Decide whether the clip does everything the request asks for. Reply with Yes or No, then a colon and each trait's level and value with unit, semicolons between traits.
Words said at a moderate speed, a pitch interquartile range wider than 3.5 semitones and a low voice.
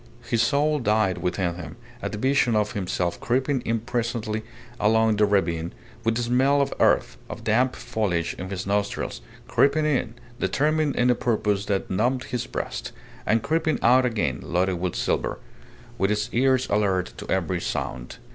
Yes: average, 165 wpm; average, 4.9 semitones; low, 110 Hz